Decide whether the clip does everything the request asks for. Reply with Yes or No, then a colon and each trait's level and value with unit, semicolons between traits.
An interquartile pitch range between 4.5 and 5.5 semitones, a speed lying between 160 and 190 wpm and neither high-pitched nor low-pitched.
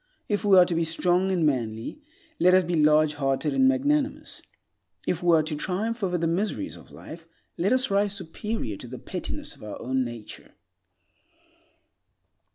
Yes: average, 5.1 semitones; average, 165 wpm; medium, 175 Hz